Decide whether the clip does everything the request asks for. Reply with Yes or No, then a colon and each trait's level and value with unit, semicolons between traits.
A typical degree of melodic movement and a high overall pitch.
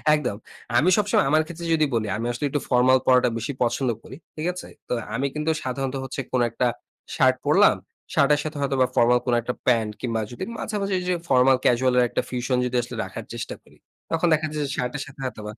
No: average, 3.5 semitones; low, 130 Hz